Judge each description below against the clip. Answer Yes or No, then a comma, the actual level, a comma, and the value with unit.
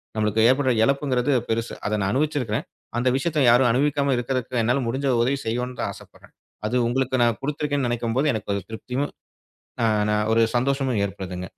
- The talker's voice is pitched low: Yes, low, 125 Hz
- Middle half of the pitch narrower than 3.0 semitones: No, average, 3.4 semitones